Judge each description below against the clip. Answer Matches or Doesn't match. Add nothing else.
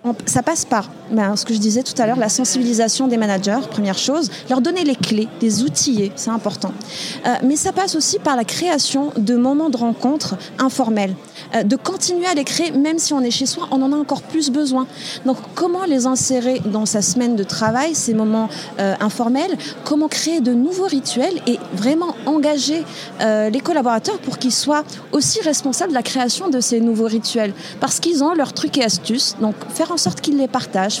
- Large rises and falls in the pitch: Doesn't match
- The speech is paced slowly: Doesn't match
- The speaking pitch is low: Doesn't match